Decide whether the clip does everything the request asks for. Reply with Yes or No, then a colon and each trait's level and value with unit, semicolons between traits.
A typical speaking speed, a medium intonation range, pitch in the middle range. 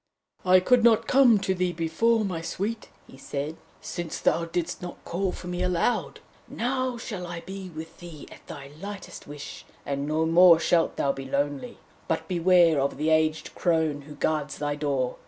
Yes: average, 180 wpm; average, 3.8 semitones; medium, 170 Hz